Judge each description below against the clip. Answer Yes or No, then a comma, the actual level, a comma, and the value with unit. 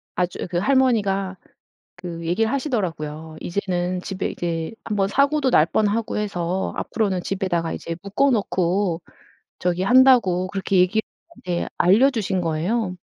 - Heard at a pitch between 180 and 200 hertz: Yes, high, 190 Hz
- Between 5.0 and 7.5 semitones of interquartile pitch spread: No, average, 3.9 semitones